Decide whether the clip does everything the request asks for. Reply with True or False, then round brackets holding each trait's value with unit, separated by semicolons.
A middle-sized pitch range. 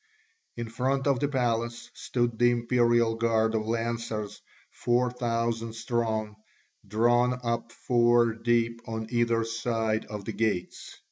False (1.1 semitones)